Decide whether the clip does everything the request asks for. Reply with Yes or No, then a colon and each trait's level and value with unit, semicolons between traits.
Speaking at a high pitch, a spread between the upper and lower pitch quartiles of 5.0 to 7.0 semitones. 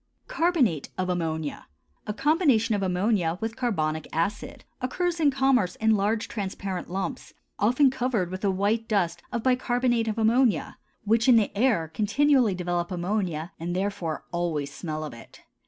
Yes: high, 205 Hz; wide, 5.6 semitones